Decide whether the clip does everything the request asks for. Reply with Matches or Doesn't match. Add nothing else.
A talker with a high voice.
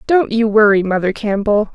Matches